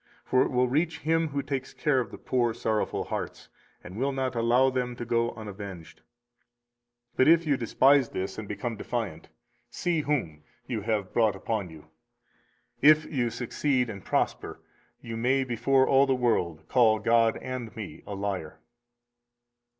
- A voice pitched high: No, low, 120 Hz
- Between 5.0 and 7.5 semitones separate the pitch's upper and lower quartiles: No, average, 3.7 semitones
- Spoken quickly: No, average, 160 wpm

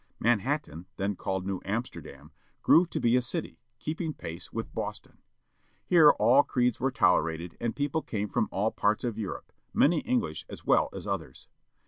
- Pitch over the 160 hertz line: No, low, 115 Hz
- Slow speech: No, average, 165 wpm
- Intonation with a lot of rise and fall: Yes, wide, 6.7 semitones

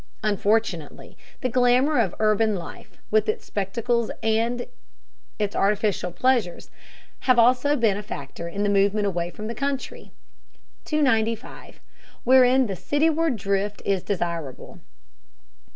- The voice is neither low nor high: No, high, 215 Hz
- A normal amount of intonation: Yes, average, 3.9 semitones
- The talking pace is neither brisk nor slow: No, slow, 120 wpm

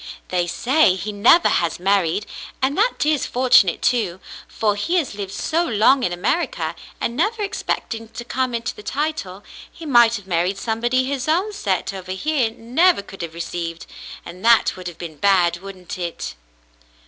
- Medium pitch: No, high, 220 Hz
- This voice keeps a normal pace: Yes, average, 170 wpm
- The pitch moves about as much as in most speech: No, wide, 6.4 semitones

